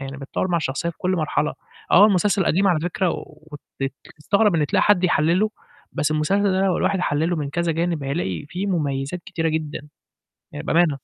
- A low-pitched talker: No, medium, 170 Hz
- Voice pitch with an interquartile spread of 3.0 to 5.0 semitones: Yes, average, 3.8 semitones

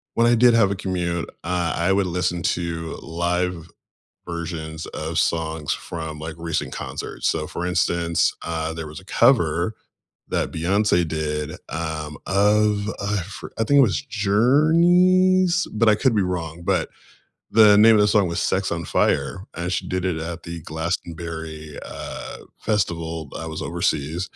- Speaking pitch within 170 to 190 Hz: No, very low, 85 Hz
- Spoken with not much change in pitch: No, average, 4.2 semitones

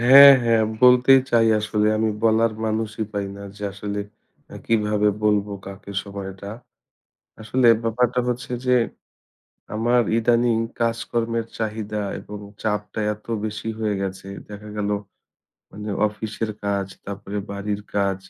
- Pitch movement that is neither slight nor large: No, narrow, 2.0 semitones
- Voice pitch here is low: Yes, low, 110 Hz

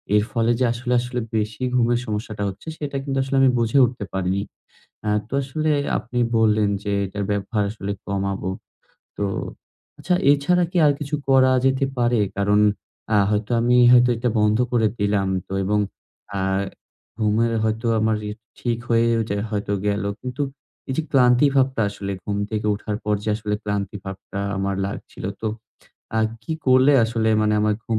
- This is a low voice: Yes, low, 110 Hz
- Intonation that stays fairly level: No, average, 3.3 semitones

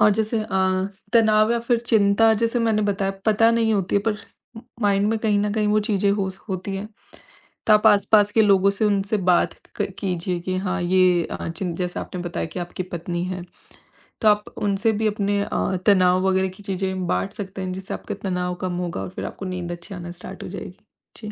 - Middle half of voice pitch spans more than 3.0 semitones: No, narrow, 2.4 semitones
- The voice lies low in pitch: No, high, 195 Hz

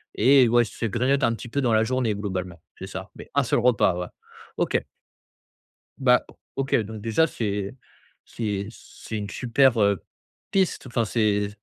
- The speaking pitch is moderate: No, low, 115 Hz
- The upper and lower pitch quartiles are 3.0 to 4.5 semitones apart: Yes, average, 3.6 semitones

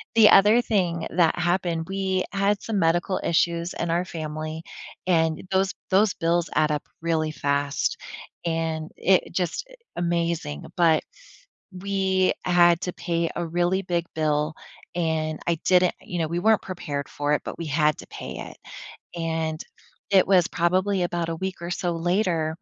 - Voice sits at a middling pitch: Yes, medium, 170 Hz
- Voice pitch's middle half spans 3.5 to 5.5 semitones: No, narrow, 2.5 semitones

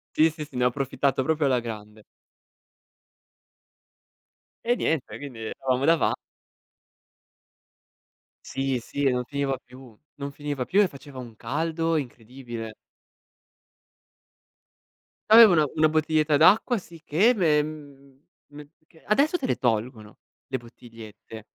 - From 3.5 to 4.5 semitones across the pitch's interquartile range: Yes, average, 4.2 semitones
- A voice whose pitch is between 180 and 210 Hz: No, medium, 140 Hz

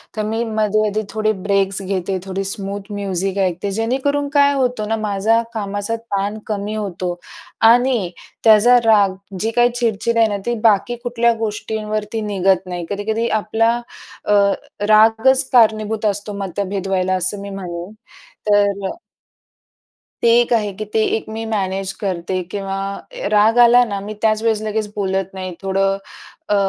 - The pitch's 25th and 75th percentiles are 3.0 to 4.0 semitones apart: No, narrow, 2.4 semitones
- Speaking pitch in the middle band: No, high, 210 Hz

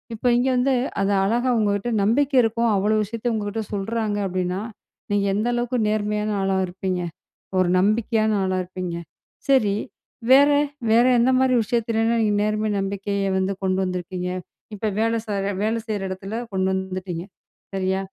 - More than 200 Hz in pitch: Yes, high, 210 Hz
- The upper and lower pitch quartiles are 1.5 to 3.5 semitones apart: Yes, average, 3.2 semitones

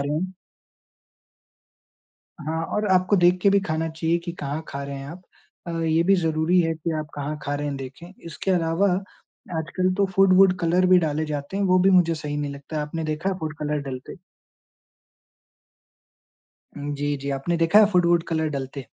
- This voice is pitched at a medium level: Yes, medium, 165 Hz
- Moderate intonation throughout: Yes, average, 3.6 semitones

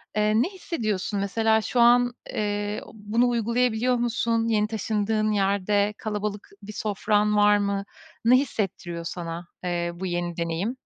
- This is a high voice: Yes, high, 210 Hz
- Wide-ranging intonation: No, narrow, 2.4 semitones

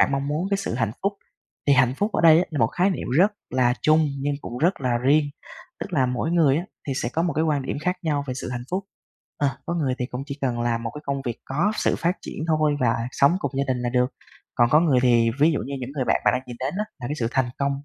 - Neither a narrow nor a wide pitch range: Yes, average, 4.2 semitones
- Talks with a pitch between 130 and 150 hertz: Yes, medium, 140 Hz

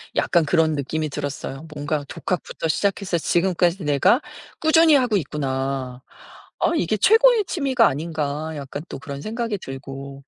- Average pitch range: No, wide, 6.6 semitones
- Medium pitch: Yes, medium, 160 Hz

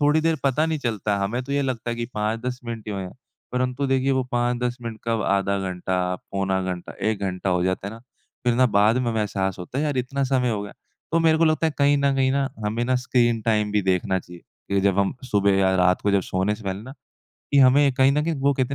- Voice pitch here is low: Yes, low, 115 Hz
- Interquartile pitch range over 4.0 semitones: Yes, average, 5.2 semitones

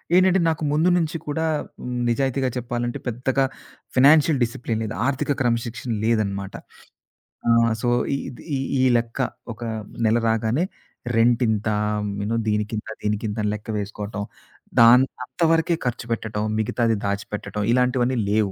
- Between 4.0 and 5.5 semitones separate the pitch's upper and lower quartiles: No, average, 3.4 semitones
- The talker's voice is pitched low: Yes, low, 115 Hz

